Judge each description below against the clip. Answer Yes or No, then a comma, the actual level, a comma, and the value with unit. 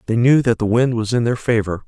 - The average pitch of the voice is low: Yes, low, 115 Hz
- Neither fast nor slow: No, fast, 290 wpm